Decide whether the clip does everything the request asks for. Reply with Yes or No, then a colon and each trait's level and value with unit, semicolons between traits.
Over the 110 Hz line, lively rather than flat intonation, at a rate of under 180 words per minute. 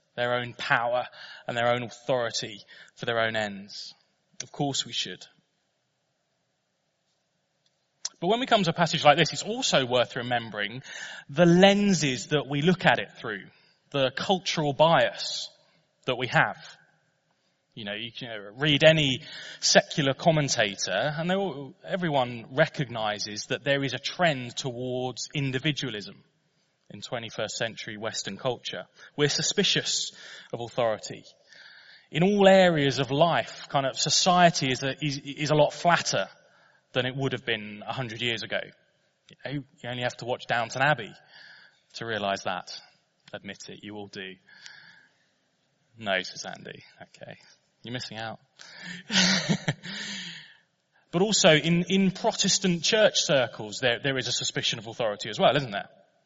Yes: medium, 140 Hz; wide, 5.9 semitones; average, 145 wpm